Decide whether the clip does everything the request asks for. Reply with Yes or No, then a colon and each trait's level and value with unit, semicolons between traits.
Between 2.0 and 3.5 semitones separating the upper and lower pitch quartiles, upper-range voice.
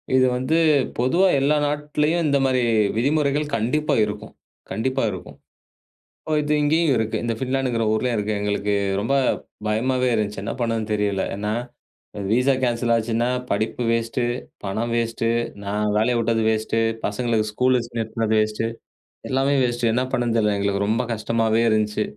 No: average, 3.2 semitones; low, 115 Hz